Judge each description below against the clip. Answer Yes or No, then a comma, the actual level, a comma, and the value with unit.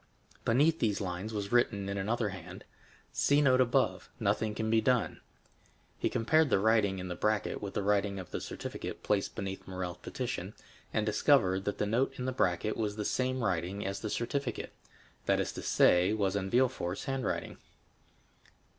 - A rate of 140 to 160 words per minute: No, average, 170 wpm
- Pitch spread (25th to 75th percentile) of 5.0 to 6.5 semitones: No, average, 3.8 semitones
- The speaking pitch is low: Yes, low, 105 Hz